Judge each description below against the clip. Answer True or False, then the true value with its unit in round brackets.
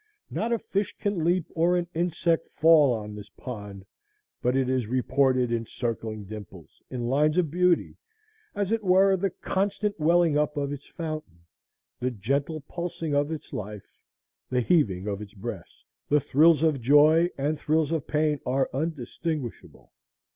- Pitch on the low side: False (150 Hz)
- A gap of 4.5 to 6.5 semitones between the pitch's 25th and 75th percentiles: True (5.3 semitones)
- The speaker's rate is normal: True (160 wpm)